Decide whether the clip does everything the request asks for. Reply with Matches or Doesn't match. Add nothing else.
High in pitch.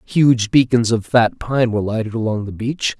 Doesn't match